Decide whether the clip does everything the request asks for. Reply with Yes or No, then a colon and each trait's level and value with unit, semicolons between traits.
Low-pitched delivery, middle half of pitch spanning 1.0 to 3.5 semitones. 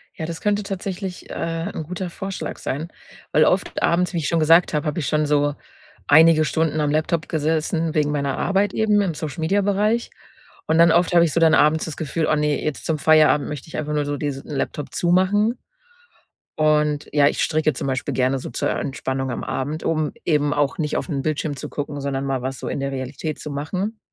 No: medium, 155 Hz; average, 2.7 semitones